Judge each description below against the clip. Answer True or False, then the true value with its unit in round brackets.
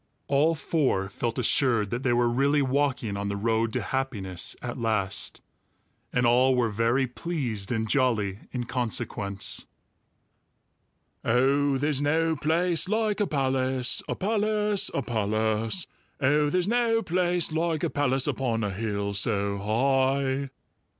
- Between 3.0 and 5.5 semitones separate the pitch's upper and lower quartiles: True (5.0 semitones)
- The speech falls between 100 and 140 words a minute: True (135 wpm)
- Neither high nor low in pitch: False (130 Hz)